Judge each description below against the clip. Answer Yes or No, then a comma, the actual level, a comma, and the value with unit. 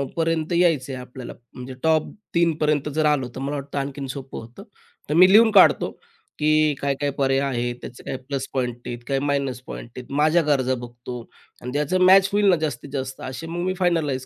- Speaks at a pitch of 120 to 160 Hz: Yes, medium, 140 Hz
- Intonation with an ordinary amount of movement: Yes, average, 3.7 semitones